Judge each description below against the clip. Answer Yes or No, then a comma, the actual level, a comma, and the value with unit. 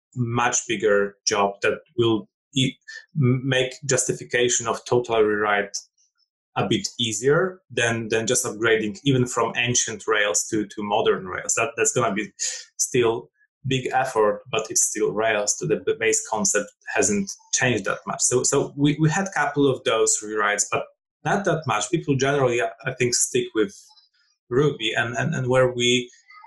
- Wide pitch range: Yes, wide, 8.9 semitones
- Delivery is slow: No, average, 165 wpm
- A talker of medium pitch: No, low, 130 Hz